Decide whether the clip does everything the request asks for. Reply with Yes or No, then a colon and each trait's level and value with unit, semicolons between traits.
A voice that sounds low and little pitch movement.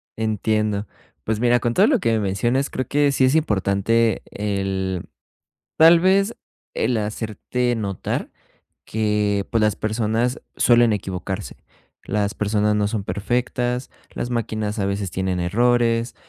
No: low, 110 Hz; average, 3.1 semitones